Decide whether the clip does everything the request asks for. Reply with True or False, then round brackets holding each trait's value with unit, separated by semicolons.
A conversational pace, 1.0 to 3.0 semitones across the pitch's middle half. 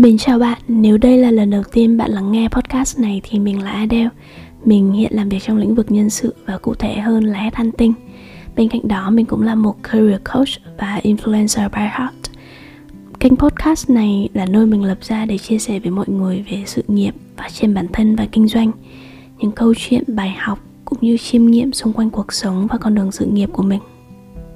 True (220 wpm; 2.4 semitones)